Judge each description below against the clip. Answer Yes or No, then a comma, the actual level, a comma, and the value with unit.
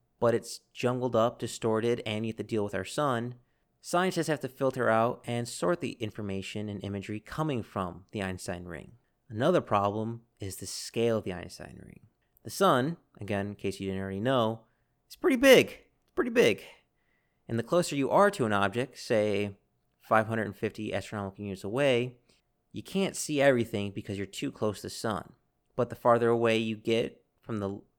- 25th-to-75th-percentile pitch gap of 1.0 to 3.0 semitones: No, average, 3.4 semitones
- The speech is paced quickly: No, average, 180 wpm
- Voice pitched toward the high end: No, low, 110 Hz